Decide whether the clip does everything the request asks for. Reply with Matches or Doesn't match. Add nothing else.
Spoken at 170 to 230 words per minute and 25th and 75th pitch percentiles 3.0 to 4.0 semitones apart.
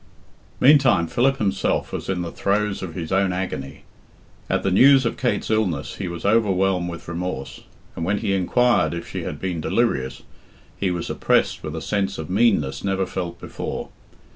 Matches